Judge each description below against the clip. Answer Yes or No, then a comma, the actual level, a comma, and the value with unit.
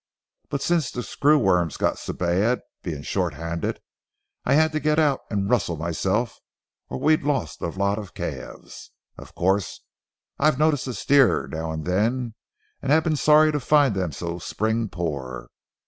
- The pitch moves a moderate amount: No, wide, 8.7 semitones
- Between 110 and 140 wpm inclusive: No, average, 175 wpm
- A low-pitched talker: Yes, low, 110 Hz